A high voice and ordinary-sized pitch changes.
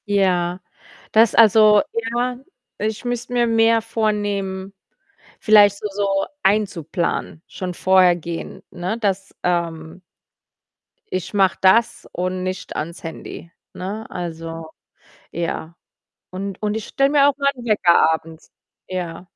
Yes: high, 195 Hz; average, 3.9 semitones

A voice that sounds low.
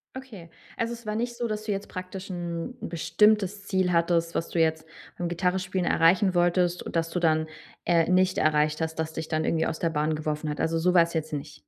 No: medium, 170 Hz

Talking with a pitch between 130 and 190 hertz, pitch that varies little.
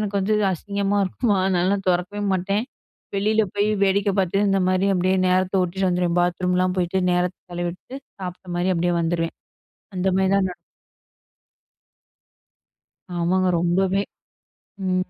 Yes: medium, 185 Hz; narrow, 1.8 semitones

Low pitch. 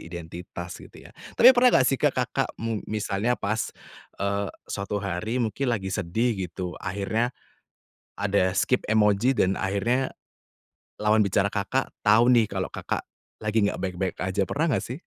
Yes: low, 105 Hz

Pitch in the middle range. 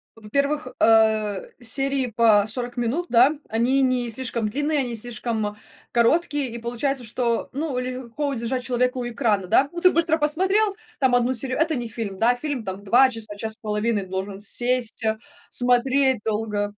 No: high, 245 Hz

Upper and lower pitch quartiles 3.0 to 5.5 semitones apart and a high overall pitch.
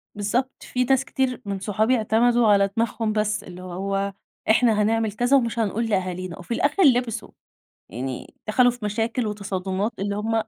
Yes: average, 3.3 semitones; high, 215 Hz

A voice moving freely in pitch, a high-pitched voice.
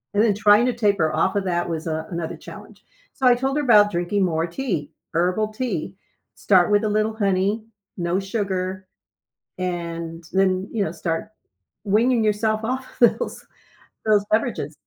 No: average, 3.7 semitones; high, 200 Hz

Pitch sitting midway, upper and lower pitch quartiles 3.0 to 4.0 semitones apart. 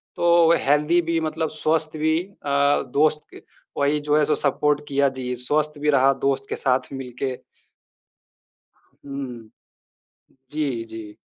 No: medium, 145 Hz; narrow, 2.4 semitones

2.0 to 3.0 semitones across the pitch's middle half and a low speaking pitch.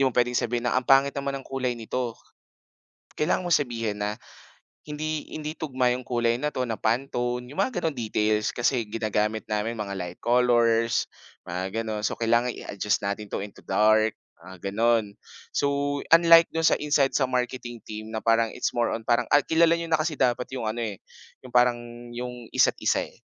No: average, 3.8 semitones; low, 120 Hz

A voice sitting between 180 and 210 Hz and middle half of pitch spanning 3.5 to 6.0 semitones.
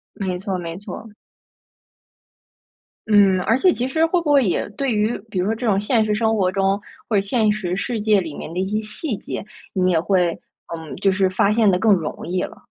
No: high, 200 Hz; average, 3.1 semitones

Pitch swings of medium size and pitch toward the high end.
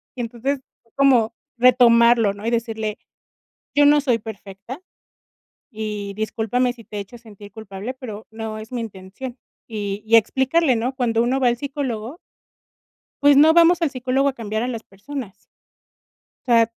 Yes: average, 3.2 semitones; high, 235 Hz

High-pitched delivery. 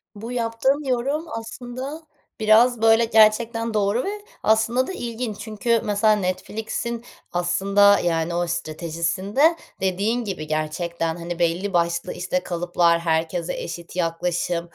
Yes: high, 205 Hz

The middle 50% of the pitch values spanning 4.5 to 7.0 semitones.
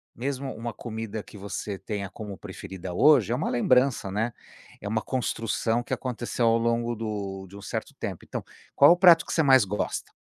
No: average, 3.8 semitones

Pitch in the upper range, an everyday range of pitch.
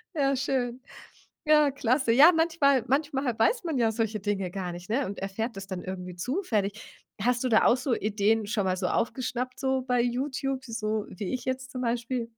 Yes: high, 240 Hz; average, 4.0 semitones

